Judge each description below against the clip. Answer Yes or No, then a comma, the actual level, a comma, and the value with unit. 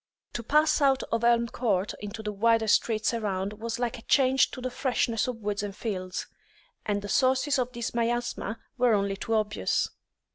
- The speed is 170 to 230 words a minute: Yes, average, 185 wpm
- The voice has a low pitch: No, high, 230 Hz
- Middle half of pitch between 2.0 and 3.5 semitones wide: Yes, average, 3.0 semitones